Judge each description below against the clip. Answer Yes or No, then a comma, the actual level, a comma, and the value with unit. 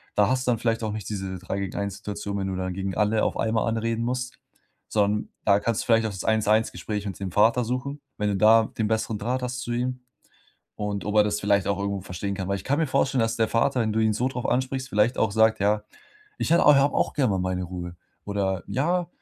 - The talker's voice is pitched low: Yes, low, 110 Hz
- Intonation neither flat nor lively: Yes, average, 3.4 semitones